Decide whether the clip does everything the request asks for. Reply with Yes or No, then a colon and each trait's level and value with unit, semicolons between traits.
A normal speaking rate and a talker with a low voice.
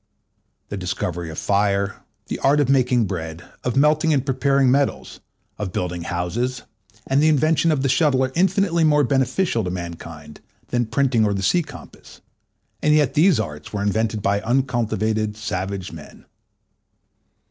Yes: average, 155 wpm; low, 120 Hz